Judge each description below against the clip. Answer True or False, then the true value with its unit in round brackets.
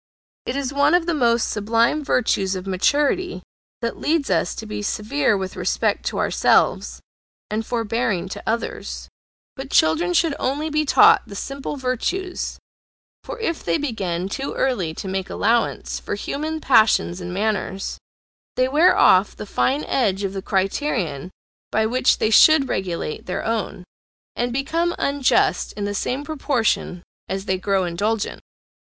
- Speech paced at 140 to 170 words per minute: True (155 wpm)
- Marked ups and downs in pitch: True (6.5 semitones)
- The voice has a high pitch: True (225 Hz)